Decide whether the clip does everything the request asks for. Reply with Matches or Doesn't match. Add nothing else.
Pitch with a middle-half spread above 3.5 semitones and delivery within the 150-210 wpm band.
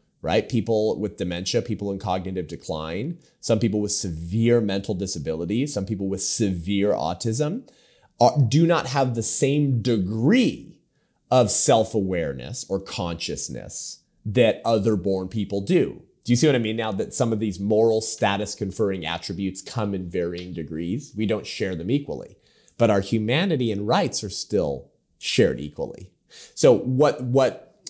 Matches